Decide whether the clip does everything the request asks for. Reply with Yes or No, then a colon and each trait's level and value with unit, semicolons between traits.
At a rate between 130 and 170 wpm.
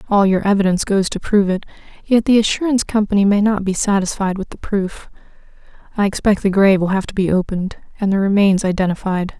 No: average, 200 wpm